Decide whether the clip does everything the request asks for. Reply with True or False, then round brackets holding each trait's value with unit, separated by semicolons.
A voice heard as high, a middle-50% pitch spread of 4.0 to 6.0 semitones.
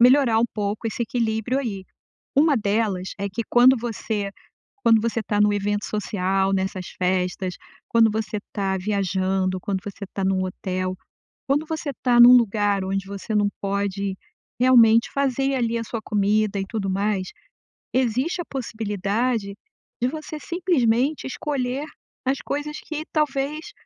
True (220 Hz; 4.4 semitones)